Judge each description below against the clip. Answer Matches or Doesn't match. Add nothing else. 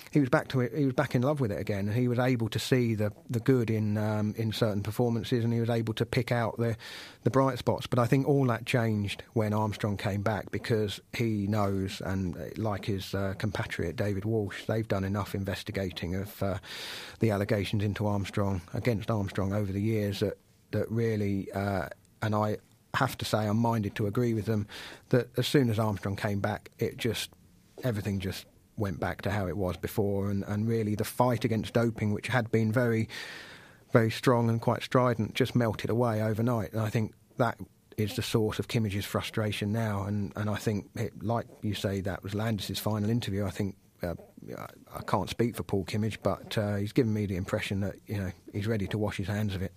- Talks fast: Matches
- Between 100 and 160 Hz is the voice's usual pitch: Matches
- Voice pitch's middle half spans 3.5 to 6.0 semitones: Doesn't match